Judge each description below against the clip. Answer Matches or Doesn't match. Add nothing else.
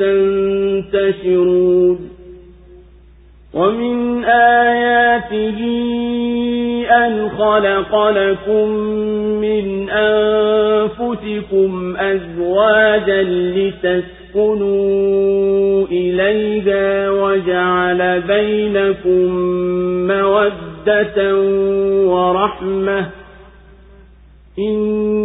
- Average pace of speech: Doesn't match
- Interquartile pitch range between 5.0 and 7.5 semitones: Doesn't match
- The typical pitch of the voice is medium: Doesn't match